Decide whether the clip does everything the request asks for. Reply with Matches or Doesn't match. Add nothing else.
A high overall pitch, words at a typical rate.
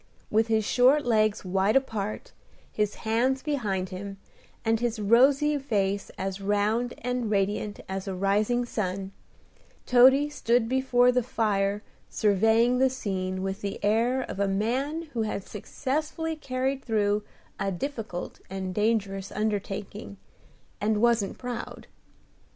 Doesn't match